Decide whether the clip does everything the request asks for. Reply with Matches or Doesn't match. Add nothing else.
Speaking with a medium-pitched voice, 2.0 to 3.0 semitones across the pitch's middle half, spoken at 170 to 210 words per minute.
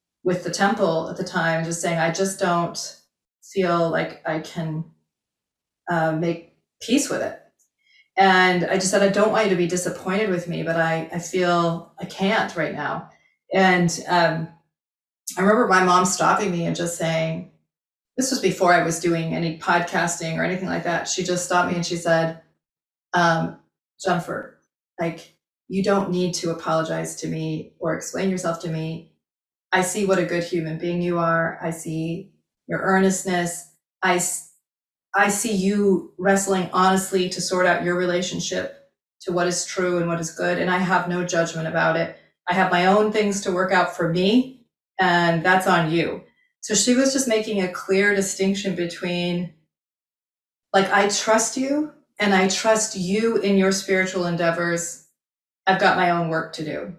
Matches